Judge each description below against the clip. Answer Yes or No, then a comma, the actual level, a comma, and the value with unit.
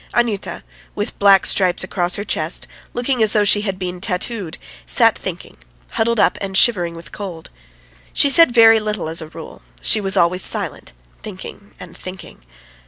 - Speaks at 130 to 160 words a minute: No, average, 170 wpm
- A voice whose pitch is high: Yes, high, 195 Hz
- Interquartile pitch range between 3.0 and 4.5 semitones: Yes, average, 3.4 semitones